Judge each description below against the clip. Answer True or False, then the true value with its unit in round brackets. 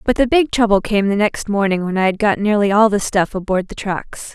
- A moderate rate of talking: False (260 wpm)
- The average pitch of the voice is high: True (205 Hz)